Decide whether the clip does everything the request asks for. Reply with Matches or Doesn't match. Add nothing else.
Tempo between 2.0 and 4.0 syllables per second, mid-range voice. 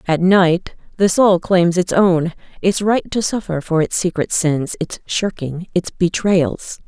Matches